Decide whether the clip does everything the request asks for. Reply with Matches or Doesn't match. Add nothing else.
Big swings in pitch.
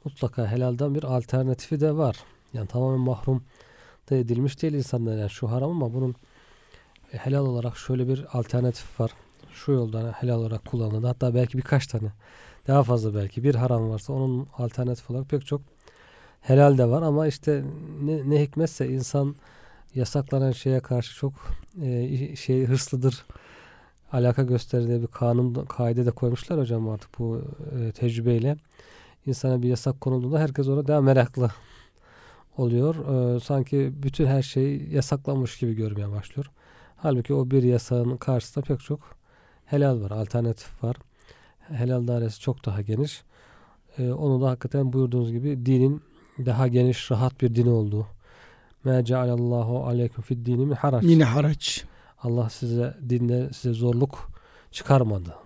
Doesn't match